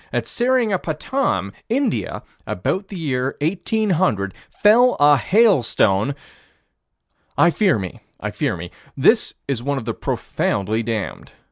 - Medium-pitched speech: Yes, medium, 150 Hz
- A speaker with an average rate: No, slow, 120 wpm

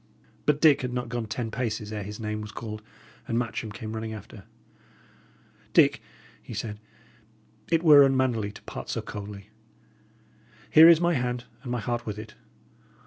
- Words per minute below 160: No, average, 165 wpm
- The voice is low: Yes, low, 115 Hz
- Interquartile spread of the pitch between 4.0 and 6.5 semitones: No, average, 3.2 semitones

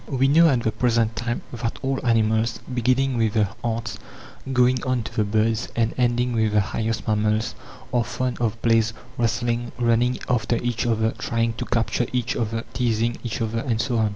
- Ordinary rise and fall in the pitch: No, narrow, 1.5 semitones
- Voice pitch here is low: Yes, low, 115 Hz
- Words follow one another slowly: No, average, 190 wpm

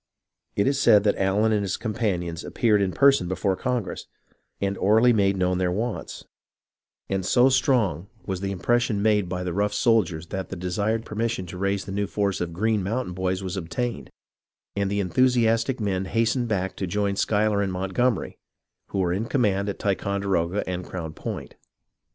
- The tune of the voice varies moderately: Yes, average, 3.2 semitones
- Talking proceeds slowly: No, average, 185 wpm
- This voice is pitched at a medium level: No, low, 100 Hz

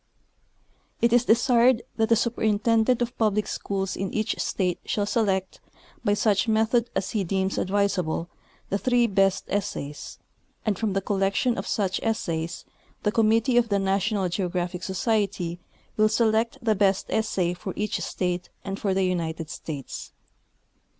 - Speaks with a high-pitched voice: Yes, high, 200 Hz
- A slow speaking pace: No, average, 150 wpm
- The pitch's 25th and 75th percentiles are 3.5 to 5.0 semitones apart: No, average, 2.9 semitones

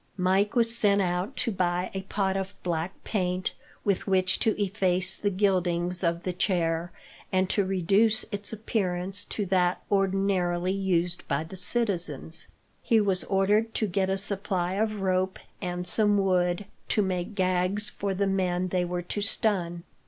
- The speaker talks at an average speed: Yes, average, 160 wpm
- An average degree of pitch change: No, narrow, 2.2 semitones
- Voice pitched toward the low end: No, high, 190 Hz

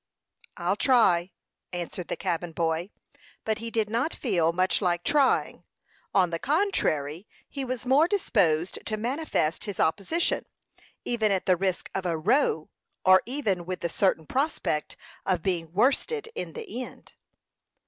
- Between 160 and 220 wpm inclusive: No, average, 150 wpm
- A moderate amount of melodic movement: No, wide, 6.9 semitones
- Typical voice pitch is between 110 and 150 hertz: No, high, 195 Hz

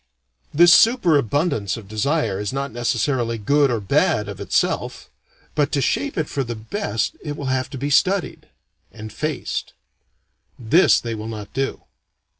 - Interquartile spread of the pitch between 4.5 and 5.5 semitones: Yes, average, 5.1 semitones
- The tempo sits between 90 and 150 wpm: No, average, 160 wpm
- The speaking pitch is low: Yes, low, 130 Hz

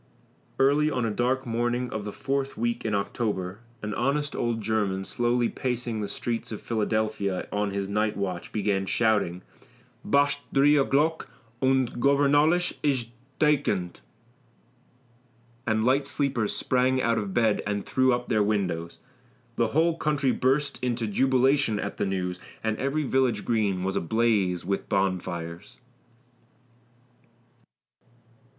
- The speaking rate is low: Yes, slow, 130 wpm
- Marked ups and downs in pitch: No, average, 4.7 semitones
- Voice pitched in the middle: No, low, 115 Hz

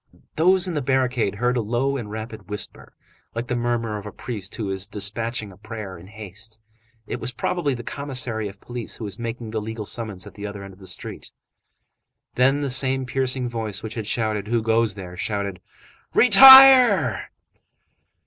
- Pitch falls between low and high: No, low, 115 Hz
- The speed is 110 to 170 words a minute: No, average, 185 wpm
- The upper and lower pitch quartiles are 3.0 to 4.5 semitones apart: Yes, average, 3.5 semitones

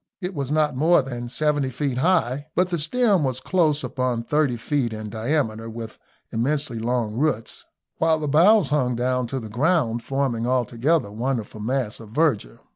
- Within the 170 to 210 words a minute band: Yes, average, 175 wpm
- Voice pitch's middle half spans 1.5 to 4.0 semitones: No, average, 4.6 semitones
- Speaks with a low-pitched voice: Yes, low, 130 Hz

